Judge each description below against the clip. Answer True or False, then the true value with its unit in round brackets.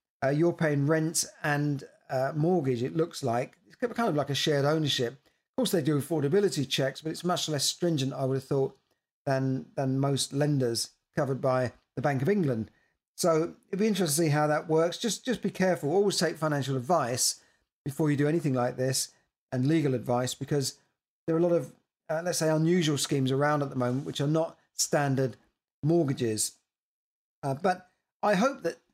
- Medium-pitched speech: True (150 Hz)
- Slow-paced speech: False (195 wpm)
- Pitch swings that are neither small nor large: True (3.9 semitones)